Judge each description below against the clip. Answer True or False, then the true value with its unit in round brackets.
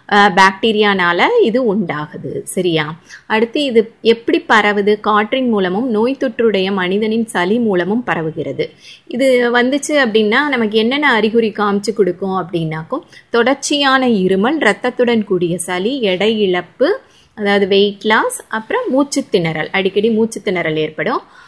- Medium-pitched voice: False (215 Hz)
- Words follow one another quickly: False (115 wpm)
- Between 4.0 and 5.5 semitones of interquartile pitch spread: True (4.3 semitones)